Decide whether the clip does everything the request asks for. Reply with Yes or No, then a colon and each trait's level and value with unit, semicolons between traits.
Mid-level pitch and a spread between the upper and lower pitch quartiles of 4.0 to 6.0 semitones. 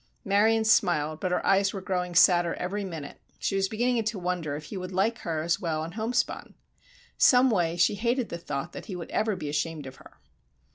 Yes: medium, 180 Hz; average, 4.4 semitones